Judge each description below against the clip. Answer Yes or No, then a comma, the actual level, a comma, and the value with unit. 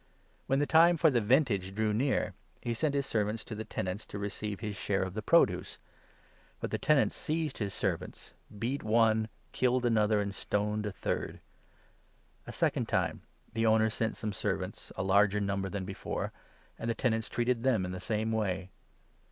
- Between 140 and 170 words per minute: No, average, 190 wpm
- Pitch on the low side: Yes, low, 110 Hz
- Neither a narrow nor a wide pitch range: Yes, average, 3.0 semitones